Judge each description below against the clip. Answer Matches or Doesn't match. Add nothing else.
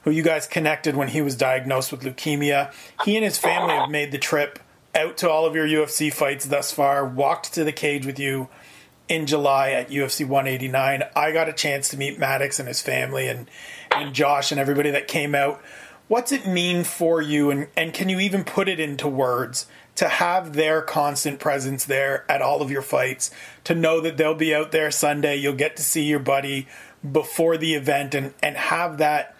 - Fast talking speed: Matches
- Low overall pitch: Doesn't match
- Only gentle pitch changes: Matches